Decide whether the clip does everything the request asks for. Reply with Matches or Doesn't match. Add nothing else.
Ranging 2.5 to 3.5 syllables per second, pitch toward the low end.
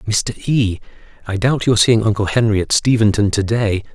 Doesn't match